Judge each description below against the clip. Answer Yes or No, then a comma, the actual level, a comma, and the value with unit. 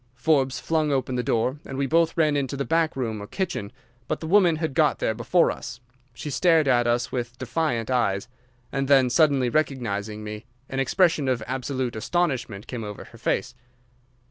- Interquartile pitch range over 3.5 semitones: Yes, average, 4.6 semitones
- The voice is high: No, low, 130 Hz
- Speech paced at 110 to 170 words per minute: No, average, 185 wpm